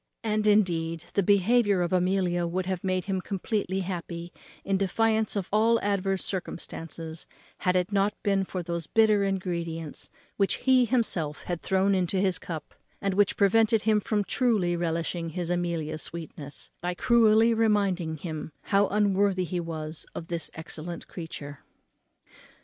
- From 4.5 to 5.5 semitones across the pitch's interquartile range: No, average, 3.2 semitones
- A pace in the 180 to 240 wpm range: No, average, 150 wpm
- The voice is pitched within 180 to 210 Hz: Yes, medium, 185 Hz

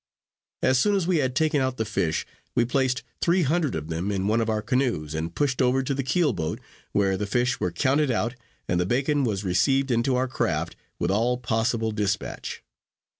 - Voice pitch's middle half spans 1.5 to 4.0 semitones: No, average, 5.0 semitones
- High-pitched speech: No, low, 120 Hz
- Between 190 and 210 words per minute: Yes, fast, 205 wpm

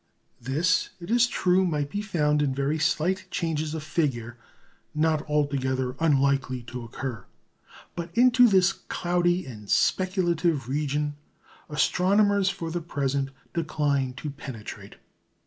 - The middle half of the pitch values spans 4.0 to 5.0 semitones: Yes, average, 4.4 semitones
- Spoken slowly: Yes, slow, 125 wpm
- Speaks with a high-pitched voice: No, medium, 150 Hz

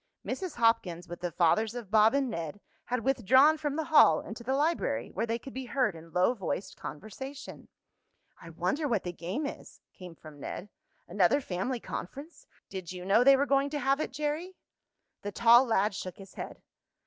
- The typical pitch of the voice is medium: No, high, 230 Hz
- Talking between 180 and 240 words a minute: Yes, average, 190 wpm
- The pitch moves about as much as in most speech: No, wide, 7.1 semitones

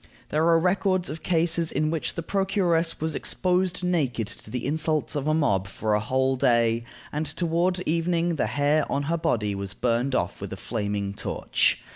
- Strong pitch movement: Yes, wide, 5.8 semitones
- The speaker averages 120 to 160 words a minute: No, average, 185 wpm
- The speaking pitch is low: No, medium, 155 Hz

